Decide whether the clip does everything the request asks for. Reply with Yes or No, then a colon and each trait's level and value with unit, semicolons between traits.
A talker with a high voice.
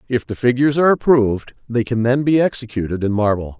No: low, 120 Hz